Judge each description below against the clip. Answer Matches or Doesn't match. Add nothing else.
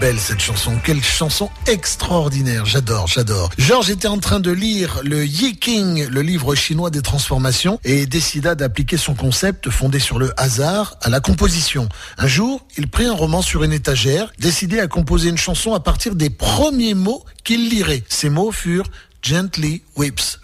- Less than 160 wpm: Doesn't match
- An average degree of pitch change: Doesn't match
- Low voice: Doesn't match